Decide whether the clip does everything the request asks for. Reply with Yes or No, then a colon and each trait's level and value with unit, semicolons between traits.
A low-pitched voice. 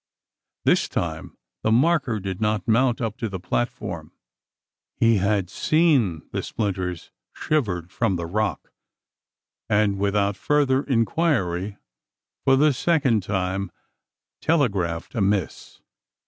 Yes: low, 105 Hz